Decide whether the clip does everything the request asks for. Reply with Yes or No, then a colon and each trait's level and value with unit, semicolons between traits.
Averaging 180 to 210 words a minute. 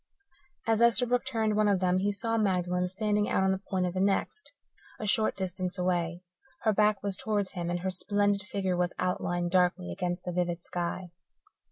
Yes: average, 190 wpm